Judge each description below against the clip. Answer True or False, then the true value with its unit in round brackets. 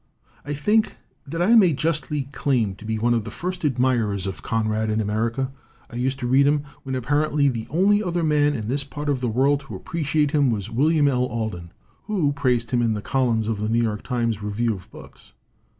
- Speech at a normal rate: False (215 wpm)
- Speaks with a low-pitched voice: True (130 Hz)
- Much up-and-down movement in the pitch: False (4.6 semitones)